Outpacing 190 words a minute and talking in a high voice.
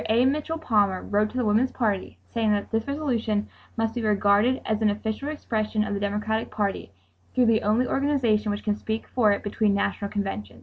Yes: average, 200 wpm; high, 215 Hz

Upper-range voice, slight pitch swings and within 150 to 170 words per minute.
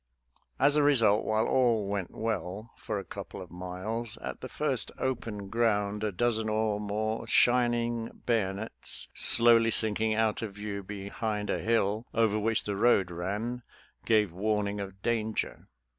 No: low, 110 Hz; narrow, 2.3 semitones; average, 160 wpm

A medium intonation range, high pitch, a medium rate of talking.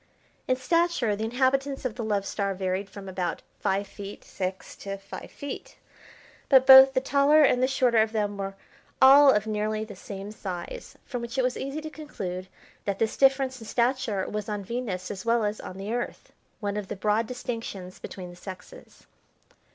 Yes: average, 4.8 semitones; high, 220 Hz; average, 190 wpm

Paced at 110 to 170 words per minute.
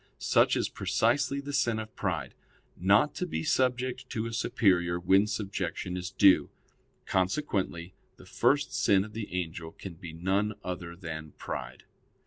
Yes: average, 150 wpm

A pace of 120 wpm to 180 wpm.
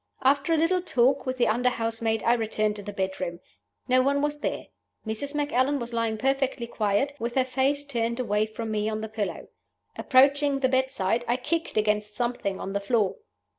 No: average, 190 wpm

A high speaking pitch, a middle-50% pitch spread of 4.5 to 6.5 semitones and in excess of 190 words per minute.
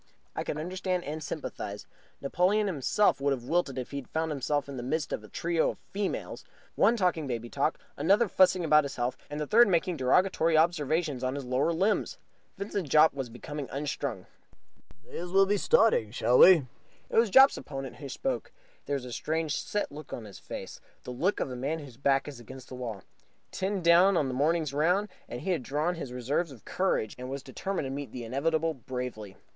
No: medium, 150 Hz; average, 5.3 semitones; fast, 205 wpm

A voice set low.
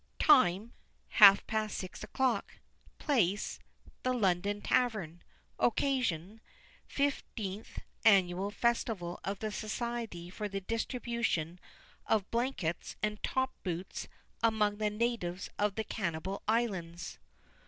No: high, 210 Hz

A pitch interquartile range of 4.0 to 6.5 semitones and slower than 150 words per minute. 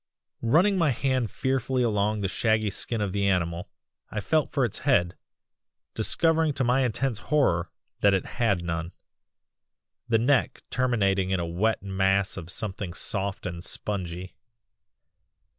Yes: average, 5.2 semitones; average, 140 wpm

